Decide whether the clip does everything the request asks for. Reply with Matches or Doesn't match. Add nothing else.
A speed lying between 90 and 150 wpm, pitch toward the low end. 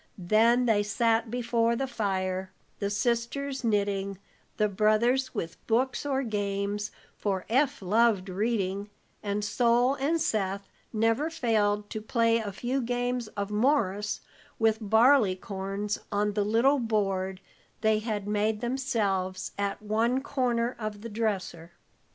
Doesn't match